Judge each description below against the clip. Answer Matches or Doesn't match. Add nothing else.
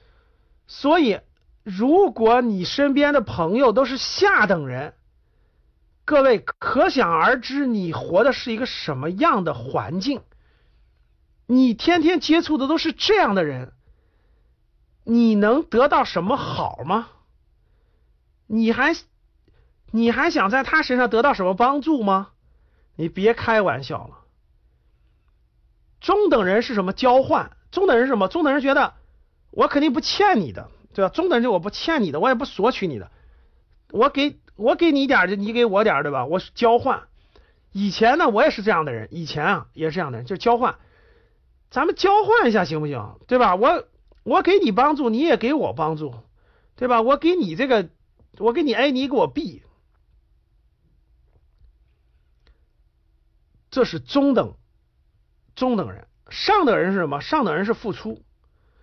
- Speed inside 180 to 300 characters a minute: Matches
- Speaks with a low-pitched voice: Doesn't match